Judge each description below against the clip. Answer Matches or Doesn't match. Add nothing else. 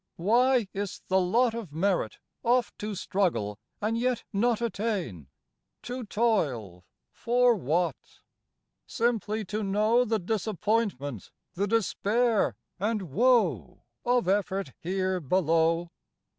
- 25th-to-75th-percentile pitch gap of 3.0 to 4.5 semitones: Doesn't match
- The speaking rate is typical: Doesn't match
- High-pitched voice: Matches